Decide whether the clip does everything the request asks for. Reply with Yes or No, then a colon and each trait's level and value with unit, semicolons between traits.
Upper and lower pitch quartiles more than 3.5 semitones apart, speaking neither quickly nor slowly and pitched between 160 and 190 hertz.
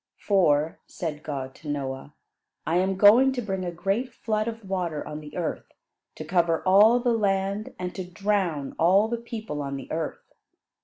Yes: average, 5.2 semitones; average, 175 wpm; medium, 185 Hz